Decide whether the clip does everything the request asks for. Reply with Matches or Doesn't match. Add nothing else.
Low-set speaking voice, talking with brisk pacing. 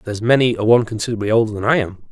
Matches